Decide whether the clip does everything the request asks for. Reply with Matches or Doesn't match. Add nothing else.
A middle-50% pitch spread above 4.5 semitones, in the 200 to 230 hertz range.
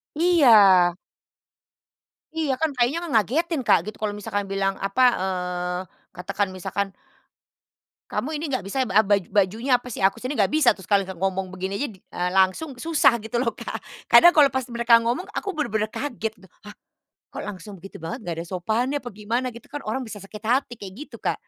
Matches